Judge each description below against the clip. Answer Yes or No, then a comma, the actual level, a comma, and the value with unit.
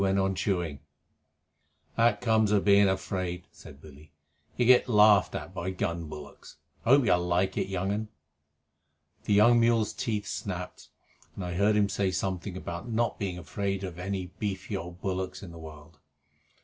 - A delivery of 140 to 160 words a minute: No, average, 175 wpm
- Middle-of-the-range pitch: No, very low, 95 Hz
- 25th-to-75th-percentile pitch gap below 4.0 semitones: Yes, average, 2.8 semitones